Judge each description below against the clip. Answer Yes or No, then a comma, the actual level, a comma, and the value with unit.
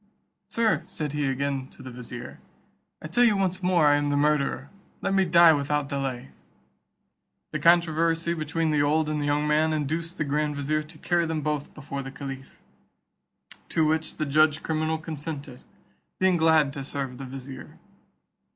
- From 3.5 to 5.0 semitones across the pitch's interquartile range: No, narrow, 2.5 semitones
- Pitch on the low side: No, medium, 150 Hz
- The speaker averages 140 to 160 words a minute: No, average, 170 wpm